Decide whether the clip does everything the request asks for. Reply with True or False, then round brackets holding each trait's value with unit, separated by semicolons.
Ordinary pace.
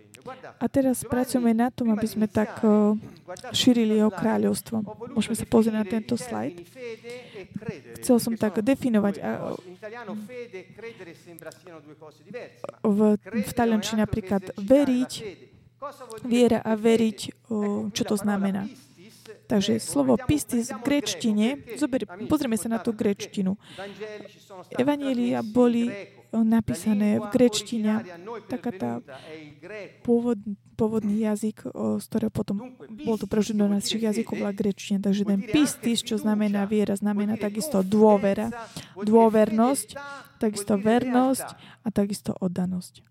False (105 wpm)